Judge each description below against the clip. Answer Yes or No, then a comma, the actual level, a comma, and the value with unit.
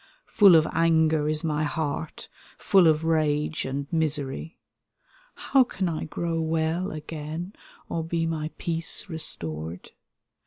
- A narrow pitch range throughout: Yes, narrow, 1.5 semitones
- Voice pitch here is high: No, medium, 160 Hz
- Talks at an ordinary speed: No, slow, 125 wpm